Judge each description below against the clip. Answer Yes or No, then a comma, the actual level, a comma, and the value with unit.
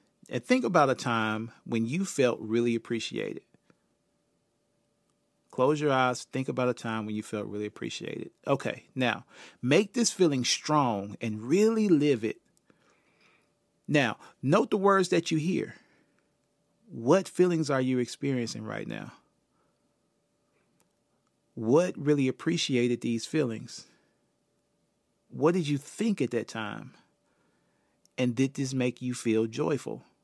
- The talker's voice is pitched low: Yes, low, 130 Hz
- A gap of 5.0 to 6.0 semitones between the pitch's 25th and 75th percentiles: Yes, wide, 5.6 semitones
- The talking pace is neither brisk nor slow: No, slow, 130 wpm